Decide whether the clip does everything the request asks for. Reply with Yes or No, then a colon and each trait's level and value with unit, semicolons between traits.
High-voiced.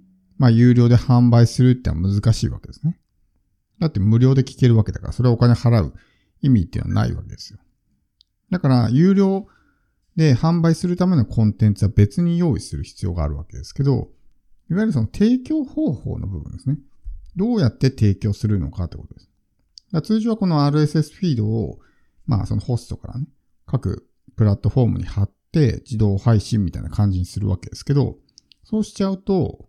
No: low, 115 Hz